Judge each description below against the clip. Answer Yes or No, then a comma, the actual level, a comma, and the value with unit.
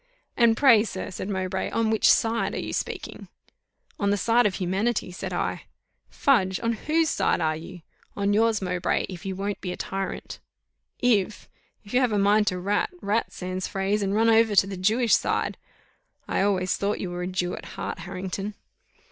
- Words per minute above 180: Yes, average, 190 wpm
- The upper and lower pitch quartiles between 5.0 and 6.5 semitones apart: No, average, 3.2 semitones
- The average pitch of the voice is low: No, high, 200 Hz